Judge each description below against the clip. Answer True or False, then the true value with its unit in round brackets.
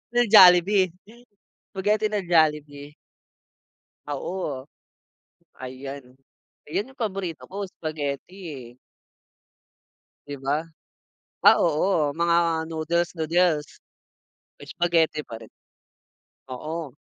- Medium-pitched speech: True (160 Hz)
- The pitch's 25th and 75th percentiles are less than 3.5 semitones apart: False (4.1 semitones)